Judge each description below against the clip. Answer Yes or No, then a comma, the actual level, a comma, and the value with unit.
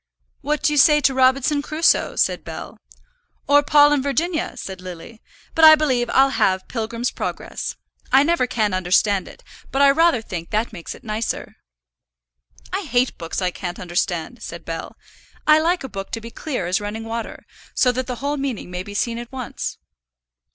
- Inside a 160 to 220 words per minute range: Yes, average, 185 wpm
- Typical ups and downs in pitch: No, wide, 6.0 semitones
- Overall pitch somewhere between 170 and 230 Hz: No, high, 245 Hz